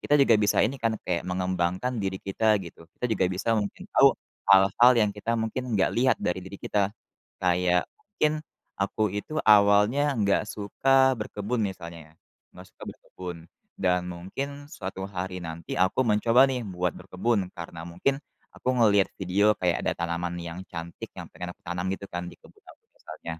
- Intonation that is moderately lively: Yes, average, 3.8 semitones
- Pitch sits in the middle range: No, very low, 95 Hz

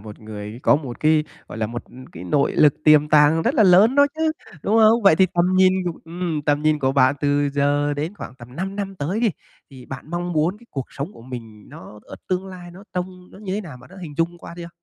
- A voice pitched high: No, medium, 155 Hz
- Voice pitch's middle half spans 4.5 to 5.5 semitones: Yes, average, 5.1 semitones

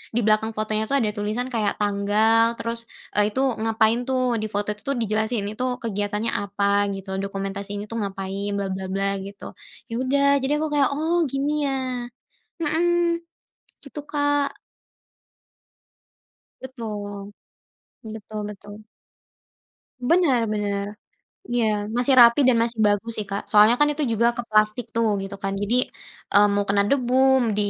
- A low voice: No, high, 220 Hz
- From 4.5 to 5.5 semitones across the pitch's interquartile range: No, average, 3.9 semitones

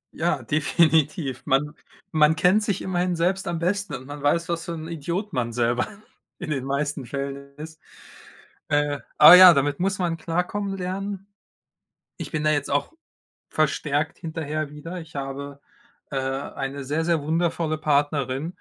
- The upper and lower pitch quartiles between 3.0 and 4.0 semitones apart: Yes, average, 3.4 semitones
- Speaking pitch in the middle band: Yes, medium, 155 Hz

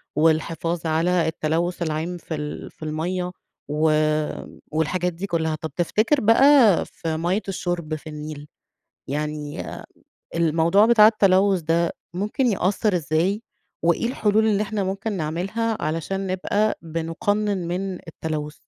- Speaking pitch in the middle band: Yes, medium, 175 Hz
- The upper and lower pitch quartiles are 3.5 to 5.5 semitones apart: Yes, average, 4.0 semitones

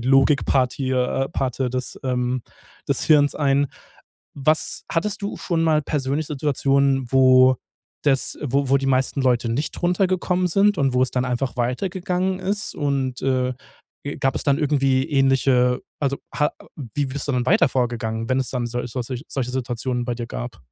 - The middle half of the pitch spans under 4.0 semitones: Yes, average, 2.7 semitones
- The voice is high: No, low, 135 Hz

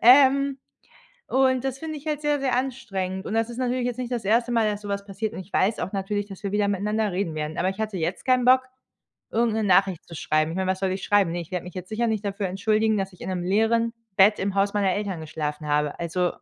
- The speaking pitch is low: No, high, 205 Hz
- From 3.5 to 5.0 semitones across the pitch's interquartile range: Yes, average, 3.9 semitones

